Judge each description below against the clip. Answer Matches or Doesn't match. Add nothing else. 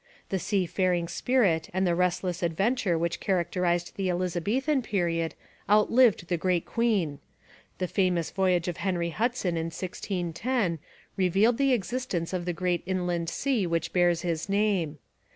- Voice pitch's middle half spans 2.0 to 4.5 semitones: Matches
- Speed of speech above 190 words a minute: Doesn't match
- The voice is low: Doesn't match